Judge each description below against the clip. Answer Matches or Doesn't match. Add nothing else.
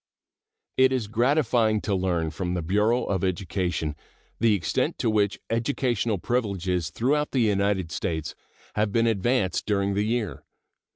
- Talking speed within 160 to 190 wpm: Doesn't match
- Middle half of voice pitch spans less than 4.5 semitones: Matches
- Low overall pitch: Matches